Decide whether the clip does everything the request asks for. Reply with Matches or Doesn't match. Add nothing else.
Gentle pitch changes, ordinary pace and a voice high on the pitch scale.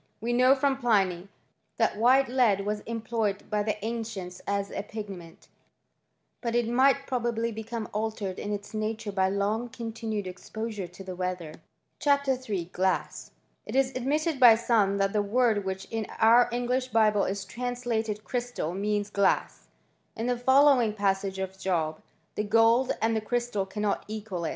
Doesn't match